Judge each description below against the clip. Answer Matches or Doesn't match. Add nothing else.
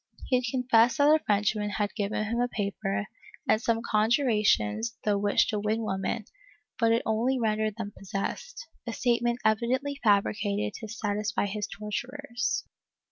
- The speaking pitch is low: Doesn't match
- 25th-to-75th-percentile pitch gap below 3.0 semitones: Matches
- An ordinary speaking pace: Matches